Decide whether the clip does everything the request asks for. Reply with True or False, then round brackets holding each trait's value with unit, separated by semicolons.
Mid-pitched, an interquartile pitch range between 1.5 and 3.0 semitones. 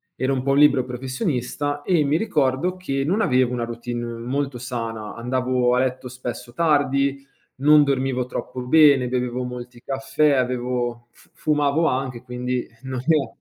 False (130 Hz; 2.4 semitones)